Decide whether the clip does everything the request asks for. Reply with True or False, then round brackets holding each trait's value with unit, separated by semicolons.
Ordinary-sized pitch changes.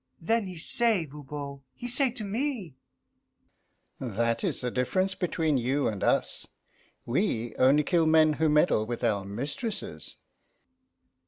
False (7.1 semitones)